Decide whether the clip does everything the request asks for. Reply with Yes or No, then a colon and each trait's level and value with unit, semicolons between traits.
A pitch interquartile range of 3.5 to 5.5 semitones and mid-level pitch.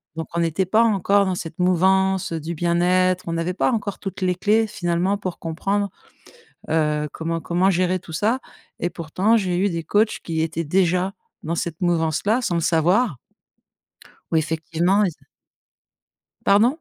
No: average, 2.9 semitones; medium, 180 Hz